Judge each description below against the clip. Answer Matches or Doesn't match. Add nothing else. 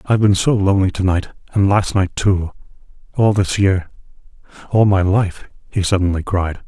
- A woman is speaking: Doesn't match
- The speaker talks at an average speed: Matches